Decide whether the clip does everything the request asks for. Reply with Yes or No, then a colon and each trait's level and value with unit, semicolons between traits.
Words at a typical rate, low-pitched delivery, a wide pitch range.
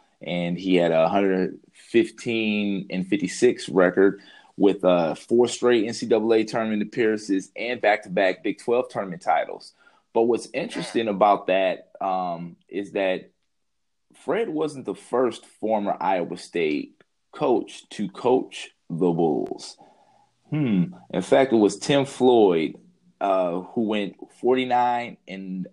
No: slow, 125 wpm; low, 110 Hz; wide, 5.9 semitones